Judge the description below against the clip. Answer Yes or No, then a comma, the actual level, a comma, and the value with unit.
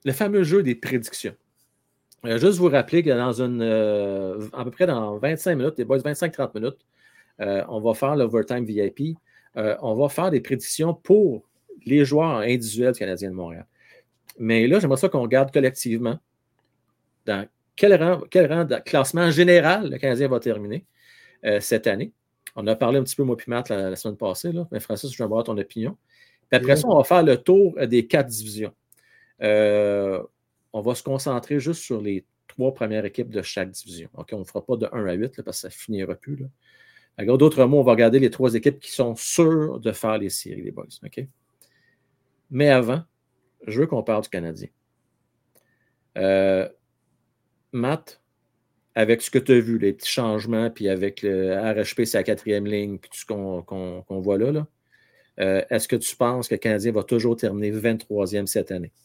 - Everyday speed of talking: Yes, average, 200 wpm